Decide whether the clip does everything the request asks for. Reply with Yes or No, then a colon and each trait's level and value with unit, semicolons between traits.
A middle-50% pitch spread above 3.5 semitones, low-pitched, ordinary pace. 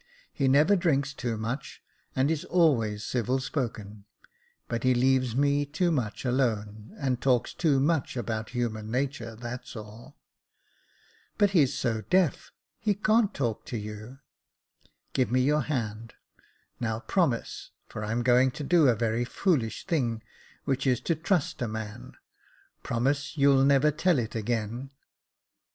Yes: average, 4.1 semitones; low, 130 Hz; average, 160 wpm